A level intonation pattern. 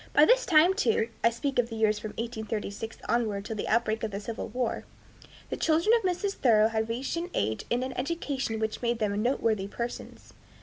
No: average, 3.8 semitones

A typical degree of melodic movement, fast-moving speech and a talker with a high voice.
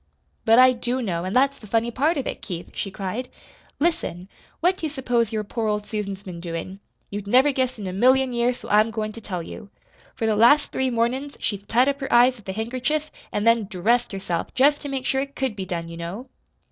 Yes: average, 4.6 semitones; fast, 235 wpm; high, 230 Hz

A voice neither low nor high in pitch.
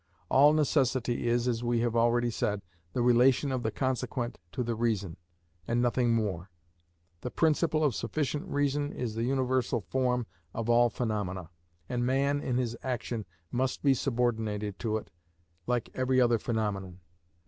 No: low, 120 Hz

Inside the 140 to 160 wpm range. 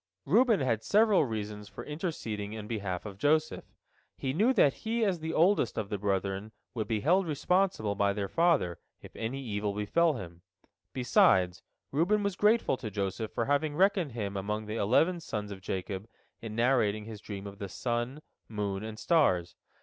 No: average, 175 wpm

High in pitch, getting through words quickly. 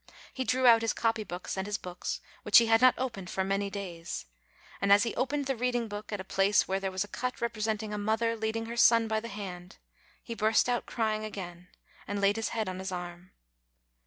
Yes: high, 215 Hz; fast, 225 wpm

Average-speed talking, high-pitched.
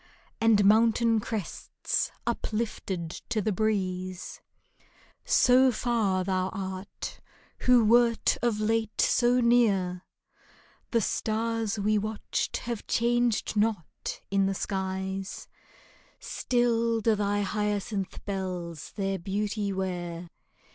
No: slow, 100 wpm; high, 210 Hz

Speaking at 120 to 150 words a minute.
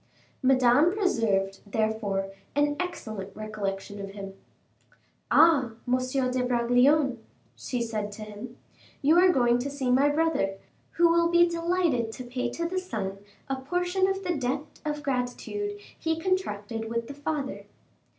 Yes: average, 145 wpm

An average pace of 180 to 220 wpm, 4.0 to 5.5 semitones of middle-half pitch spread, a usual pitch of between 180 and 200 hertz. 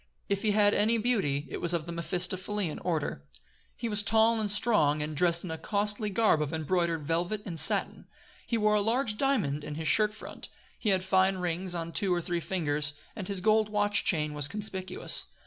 Yes: average, 200 wpm; average, 4.3 semitones; medium, 185 Hz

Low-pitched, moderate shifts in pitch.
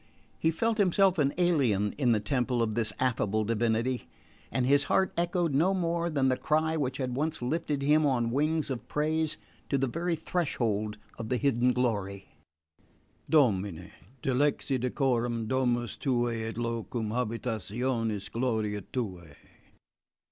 Yes: low, 125 Hz; average, 4.8 semitones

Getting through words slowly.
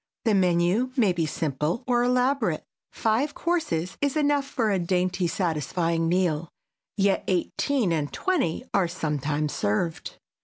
Yes: slow, 130 wpm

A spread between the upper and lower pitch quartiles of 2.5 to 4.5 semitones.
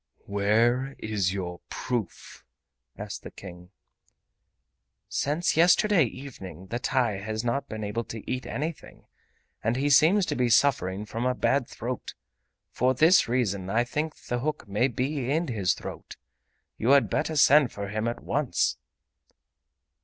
No: average, 4.9 semitones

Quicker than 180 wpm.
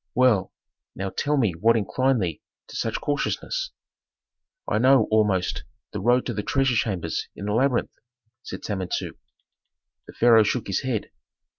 No: average, 150 wpm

